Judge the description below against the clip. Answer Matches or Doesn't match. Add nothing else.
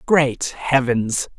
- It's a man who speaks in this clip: Matches